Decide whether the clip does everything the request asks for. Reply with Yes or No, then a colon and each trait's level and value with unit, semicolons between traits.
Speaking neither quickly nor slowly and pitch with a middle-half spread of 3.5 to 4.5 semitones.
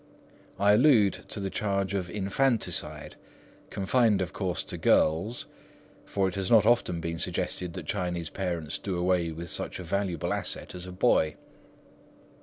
No: average, 155 wpm; average, 2.7 semitones